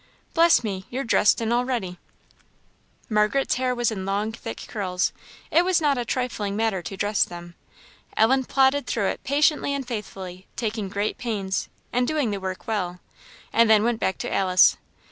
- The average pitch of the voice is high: Yes, high, 220 Hz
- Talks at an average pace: Yes, average, 175 wpm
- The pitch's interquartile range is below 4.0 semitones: No, average, 4.4 semitones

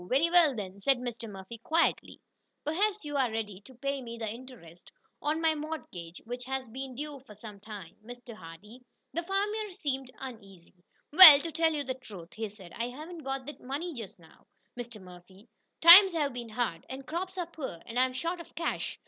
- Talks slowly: No, average, 200 wpm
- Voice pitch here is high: Yes, very high, 255 Hz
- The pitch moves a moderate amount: No, wide, 6.4 semitones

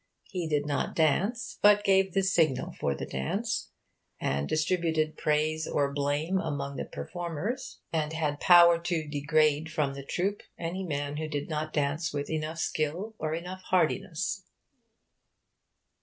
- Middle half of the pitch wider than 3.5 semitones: No, average, 3.2 semitones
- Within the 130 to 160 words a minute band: Yes, average, 145 wpm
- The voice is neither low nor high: Yes, medium, 155 Hz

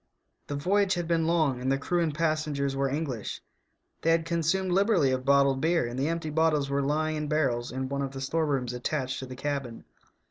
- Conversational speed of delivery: No, fast, 220 wpm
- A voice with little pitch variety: No, average, 3.4 semitones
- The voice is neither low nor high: Yes, medium, 145 Hz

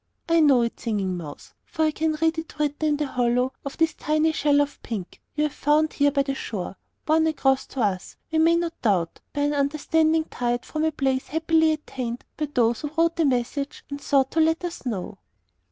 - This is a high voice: Yes, very high, 290 Hz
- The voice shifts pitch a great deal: No, average, 4.2 semitones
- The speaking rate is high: Yes, fast, 215 wpm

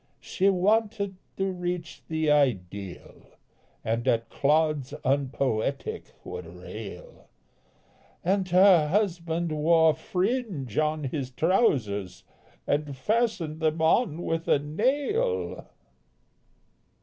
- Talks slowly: Yes, slow, 95 wpm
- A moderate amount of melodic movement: No, wide, 5.8 semitones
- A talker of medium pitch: Yes, medium, 160 Hz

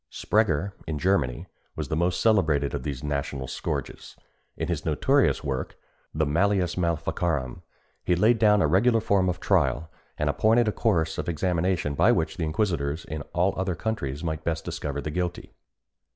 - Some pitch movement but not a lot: Yes, average, 4.7 semitones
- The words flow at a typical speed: Yes, average, 165 wpm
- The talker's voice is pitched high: No, very low, 85 Hz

